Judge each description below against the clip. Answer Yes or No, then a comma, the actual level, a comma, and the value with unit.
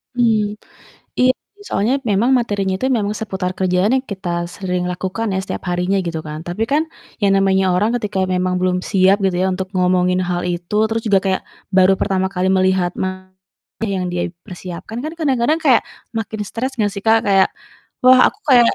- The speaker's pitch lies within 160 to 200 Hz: Yes, high, 190 Hz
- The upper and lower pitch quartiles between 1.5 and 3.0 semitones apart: No, average, 3.4 semitones